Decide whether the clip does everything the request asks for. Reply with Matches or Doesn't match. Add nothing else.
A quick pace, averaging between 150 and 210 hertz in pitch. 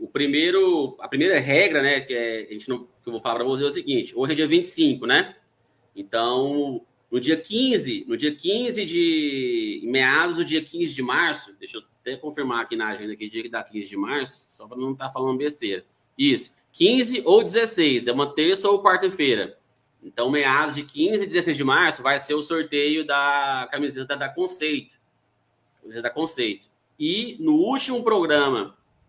Matches